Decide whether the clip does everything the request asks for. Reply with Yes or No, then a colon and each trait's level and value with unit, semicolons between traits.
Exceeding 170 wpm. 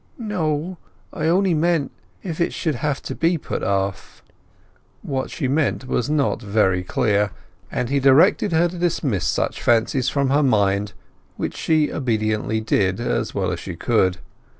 No: average, 150 wpm